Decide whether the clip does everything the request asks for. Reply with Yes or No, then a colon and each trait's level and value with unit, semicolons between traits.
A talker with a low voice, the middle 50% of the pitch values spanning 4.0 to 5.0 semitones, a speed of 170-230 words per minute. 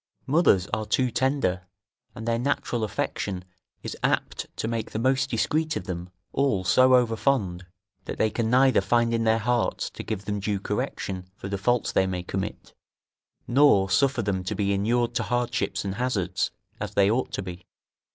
Yes: low, 110 Hz; average, 4.3 semitones; average, 180 wpm